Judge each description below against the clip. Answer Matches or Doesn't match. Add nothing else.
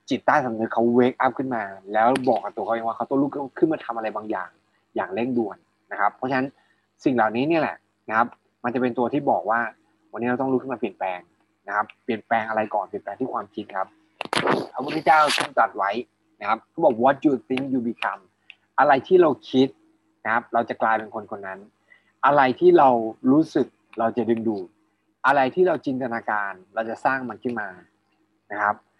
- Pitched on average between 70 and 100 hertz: Doesn't match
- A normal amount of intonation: Matches